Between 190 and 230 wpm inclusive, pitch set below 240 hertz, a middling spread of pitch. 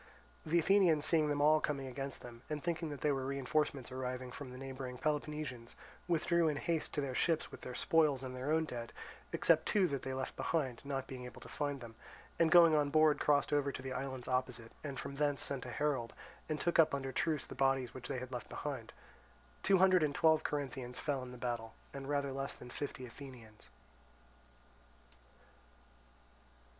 Yes: average, 195 wpm; medium, 140 Hz; average, 3.0 semitones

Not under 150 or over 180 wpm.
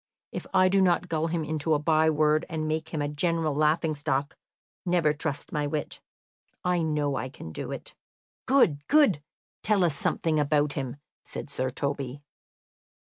Yes: average, 170 wpm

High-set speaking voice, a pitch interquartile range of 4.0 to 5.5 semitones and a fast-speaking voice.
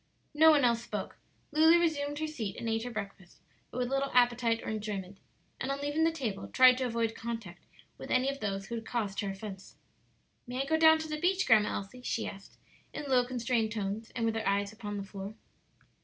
Yes: high, 235 Hz; average, 4.9 semitones; fast, 215 wpm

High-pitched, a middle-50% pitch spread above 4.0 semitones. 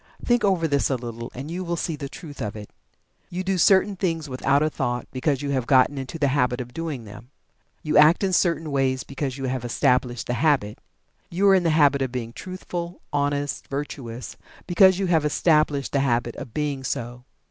No: medium, 140 Hz; average, 4.6 semitones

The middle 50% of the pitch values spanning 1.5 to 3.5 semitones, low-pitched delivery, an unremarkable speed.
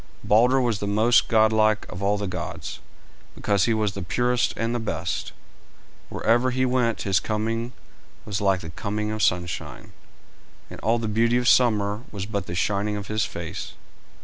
Yes: narrow, 2.5 semitones; low, 110 Hz; average, 175 wpm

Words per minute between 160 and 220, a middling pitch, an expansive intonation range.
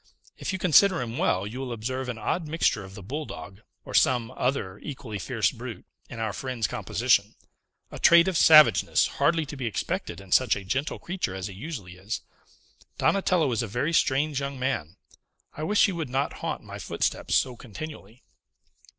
No: average, 185 wpm; low, 130 Hz; wide, 6.3 semitones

